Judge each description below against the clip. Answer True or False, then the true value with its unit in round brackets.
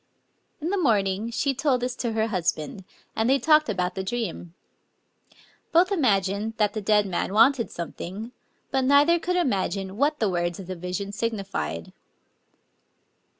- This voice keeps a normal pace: True (150 wpm)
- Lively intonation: True (5.8 semitones)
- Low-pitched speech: False (215 Hz)